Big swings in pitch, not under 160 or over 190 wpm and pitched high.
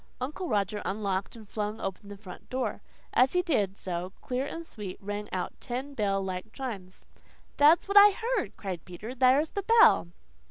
Yes: wide, 6.2 semitones; average, 175 wpm; high, 215 Hz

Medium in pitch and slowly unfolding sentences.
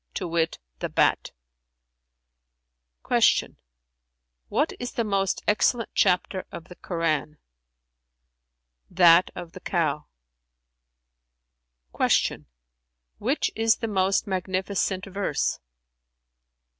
Yes: medium, 175 Hz; slow, 90 wpm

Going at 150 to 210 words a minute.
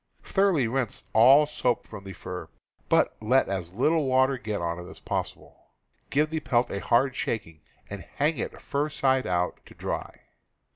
Yes: average, 180 wpm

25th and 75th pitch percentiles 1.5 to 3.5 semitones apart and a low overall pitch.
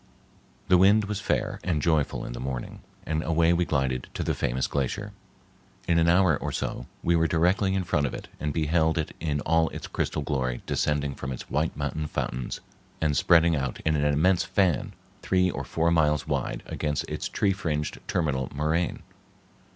Yes: average, 3.2 semitones; very low, 80 Hz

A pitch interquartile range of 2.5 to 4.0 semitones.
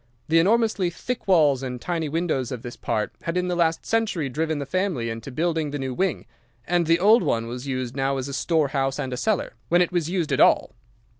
No: average, 4.9 semitones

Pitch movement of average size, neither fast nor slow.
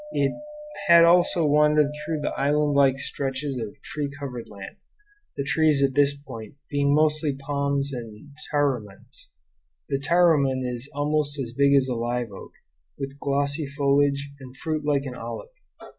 No: narrow, 1.9 semitones; average, 160 wpm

